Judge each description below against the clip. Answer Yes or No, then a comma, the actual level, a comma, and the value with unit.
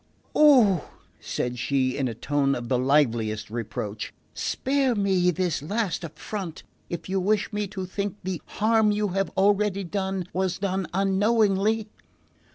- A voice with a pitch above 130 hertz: Yes, high, 190 Hz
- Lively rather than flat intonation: Yes, wide, 6.2 semitones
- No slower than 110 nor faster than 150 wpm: Yes, average, 145 wpm